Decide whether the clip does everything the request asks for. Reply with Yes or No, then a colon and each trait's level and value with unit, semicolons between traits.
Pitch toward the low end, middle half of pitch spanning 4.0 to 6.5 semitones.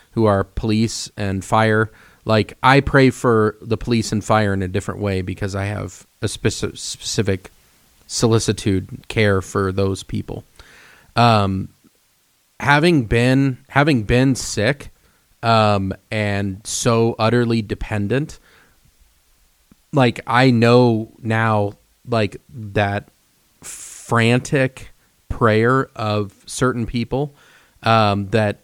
No: low, 110 Hz; average, 3.3 semitones